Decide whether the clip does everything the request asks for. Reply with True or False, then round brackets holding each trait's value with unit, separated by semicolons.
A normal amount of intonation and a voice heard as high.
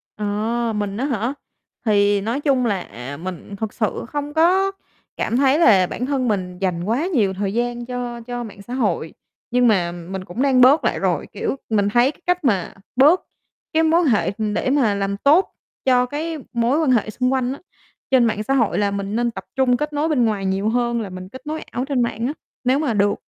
True (4.8 semitones; 235 Hz)